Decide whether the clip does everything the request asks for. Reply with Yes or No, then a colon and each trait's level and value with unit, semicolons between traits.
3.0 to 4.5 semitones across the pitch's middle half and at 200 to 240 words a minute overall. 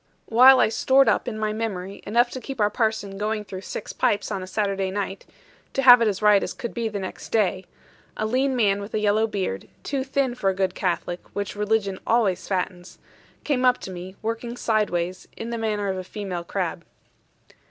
Yes: average, 3.3 semitones; fast, 205 wpm